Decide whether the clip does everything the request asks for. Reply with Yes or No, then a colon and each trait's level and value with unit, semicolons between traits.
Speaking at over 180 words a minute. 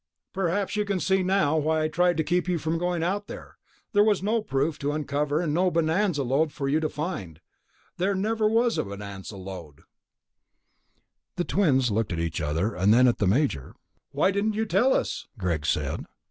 Yes: average, 195 wpm